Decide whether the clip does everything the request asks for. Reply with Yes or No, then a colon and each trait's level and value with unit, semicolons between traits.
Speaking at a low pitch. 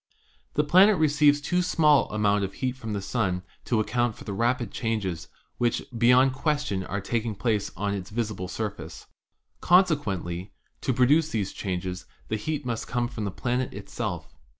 Yes: low, 115 Hz